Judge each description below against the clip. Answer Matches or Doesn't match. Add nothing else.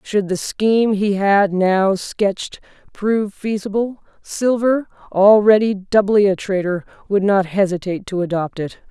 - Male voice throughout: Doesn't match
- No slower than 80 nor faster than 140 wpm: Matches